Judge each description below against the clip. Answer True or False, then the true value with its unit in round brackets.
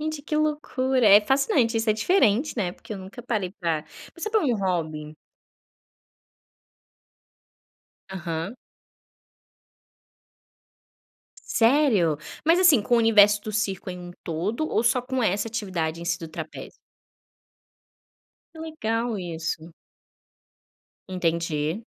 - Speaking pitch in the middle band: False (210 Hz)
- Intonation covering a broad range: True (6.7 semitones)